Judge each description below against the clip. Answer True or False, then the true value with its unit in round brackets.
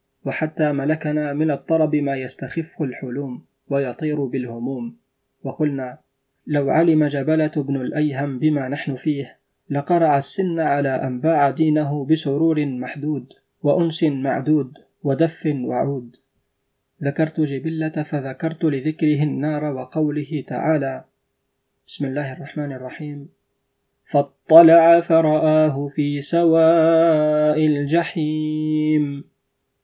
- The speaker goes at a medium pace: True (90 wpm)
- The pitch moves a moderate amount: False (2.2 semitones)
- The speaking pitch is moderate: True (150 Hz)